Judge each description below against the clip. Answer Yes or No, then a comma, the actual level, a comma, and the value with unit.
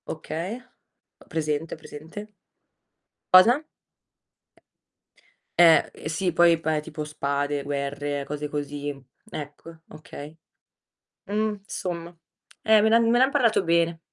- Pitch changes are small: No, average, 5.2 semitones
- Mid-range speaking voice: Yes, medium, 165 Hz